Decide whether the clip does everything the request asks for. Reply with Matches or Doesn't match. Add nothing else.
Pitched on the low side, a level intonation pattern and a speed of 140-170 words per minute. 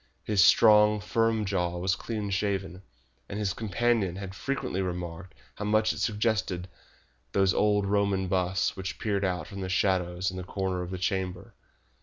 Matches